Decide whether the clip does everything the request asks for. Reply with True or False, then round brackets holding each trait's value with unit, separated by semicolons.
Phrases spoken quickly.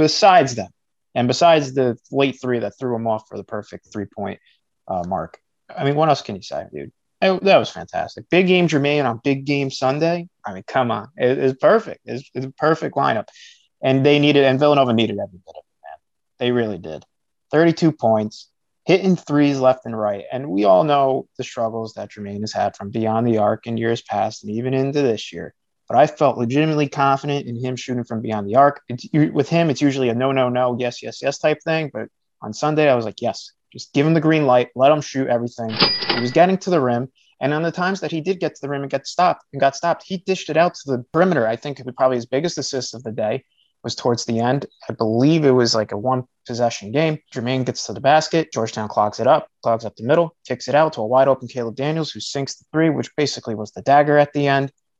True (240 wpm)